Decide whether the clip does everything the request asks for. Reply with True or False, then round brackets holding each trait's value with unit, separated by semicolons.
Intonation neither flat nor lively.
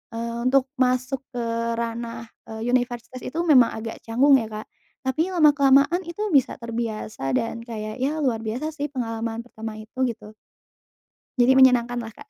True (3.1 semitones)